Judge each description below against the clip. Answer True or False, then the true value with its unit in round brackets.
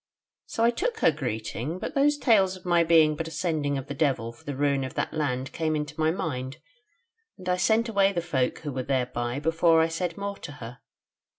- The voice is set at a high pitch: False (155 Hz)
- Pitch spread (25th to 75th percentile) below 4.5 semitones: False (5.1 semitones)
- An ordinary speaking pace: False (220 wpm)